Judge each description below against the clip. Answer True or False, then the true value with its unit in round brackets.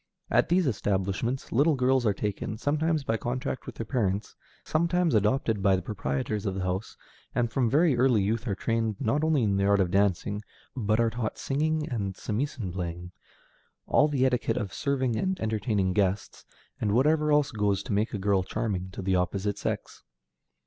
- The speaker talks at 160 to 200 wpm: True (185 wpm)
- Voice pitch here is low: True (110 Hz)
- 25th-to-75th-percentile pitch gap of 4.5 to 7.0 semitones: True (5.1 semitones)